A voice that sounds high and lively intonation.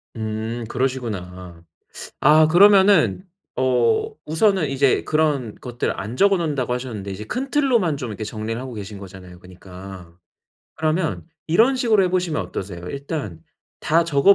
No: low, 130 Hz; wide, 8.7 semitones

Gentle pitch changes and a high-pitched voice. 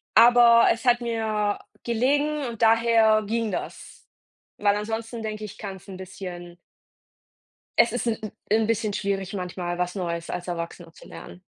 No: average, 3.6 semitones; high, 215 Hz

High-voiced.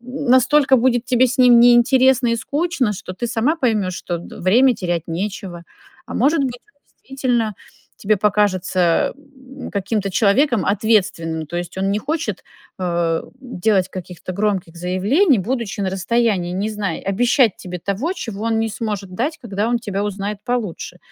Yes: high, 215 Hz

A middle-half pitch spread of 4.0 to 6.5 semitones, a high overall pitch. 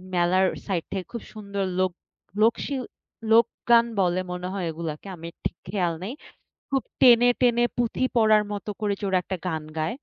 Yes: average, 4.5 semitones; high, 200 Hz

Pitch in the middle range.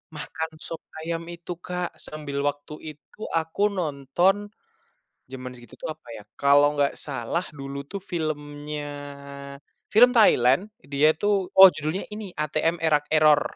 Yes: medium, 150 Hz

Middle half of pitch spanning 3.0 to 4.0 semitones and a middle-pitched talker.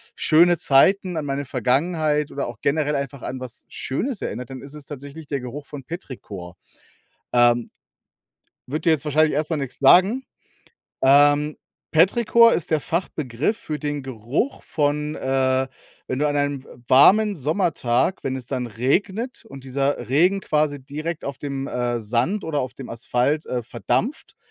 Yes: average, 3.5 semitones; medium, 145 Hz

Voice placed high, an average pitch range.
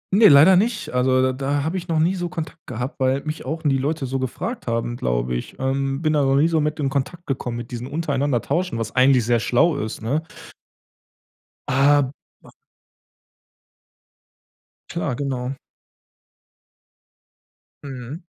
No: low, 135 Hz; average, 3.8 semitones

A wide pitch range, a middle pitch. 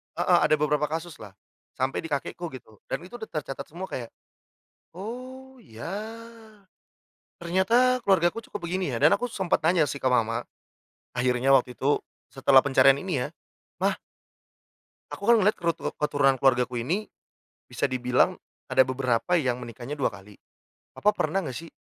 Yes: wide, 6.5 semitones; medium, 150 Hz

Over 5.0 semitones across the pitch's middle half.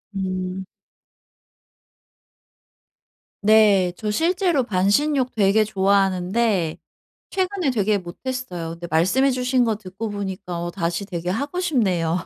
Yes: wide, 5.5 semitones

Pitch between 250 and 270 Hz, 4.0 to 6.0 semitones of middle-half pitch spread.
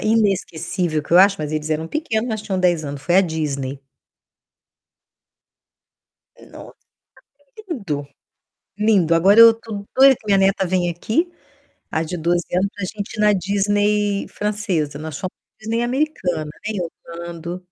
No: high, 190 Hz; average, 4.3 semitones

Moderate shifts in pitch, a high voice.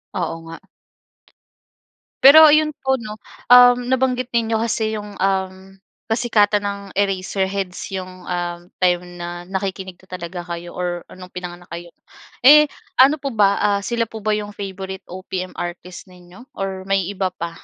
Yes: average, 3.4 semitones; high, 195 Hz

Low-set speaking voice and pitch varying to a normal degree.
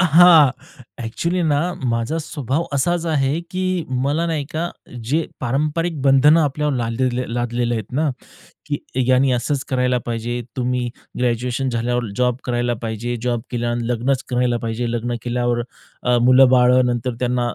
Yes: low, 125 Hz; average, 3.2 semitones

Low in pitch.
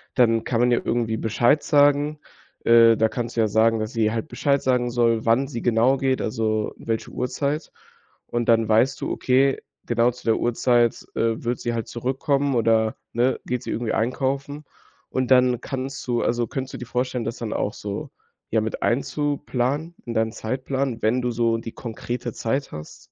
Yes: low, 120 Hz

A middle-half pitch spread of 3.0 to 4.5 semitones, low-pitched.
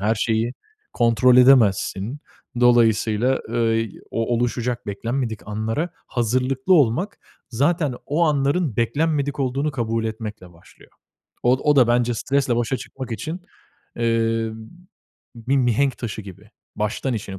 Yes: average, 3.3 semitones; low, 120 Hz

